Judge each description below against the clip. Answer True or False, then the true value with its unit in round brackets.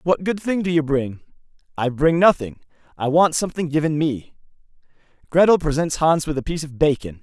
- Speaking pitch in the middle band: True (155 Hz)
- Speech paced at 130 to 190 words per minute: True (185 wpm)